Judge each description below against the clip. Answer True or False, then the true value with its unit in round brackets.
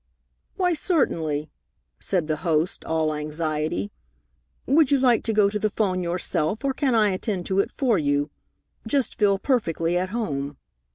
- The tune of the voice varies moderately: False (6.6 semitones)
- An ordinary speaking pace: True (160 wpm)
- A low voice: False (185 Hz)